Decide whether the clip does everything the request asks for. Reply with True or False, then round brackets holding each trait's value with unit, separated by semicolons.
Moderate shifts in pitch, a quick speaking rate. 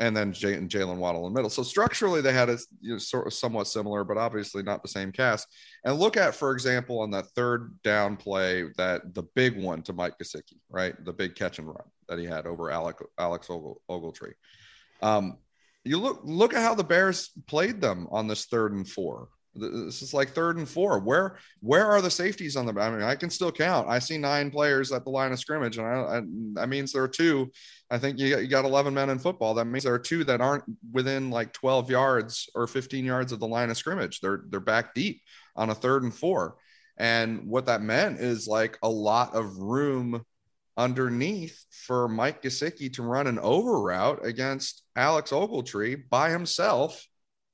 True (4.2 semitones; 215 wpm)